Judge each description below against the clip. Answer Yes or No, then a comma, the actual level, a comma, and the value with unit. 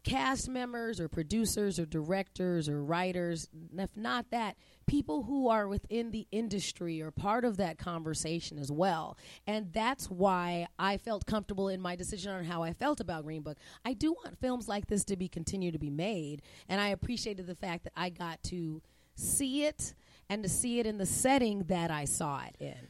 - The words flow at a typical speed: Yes, average, 195 wpm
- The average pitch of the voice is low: No, high, 190 Hz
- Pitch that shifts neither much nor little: Yes, average, 4.7 semitones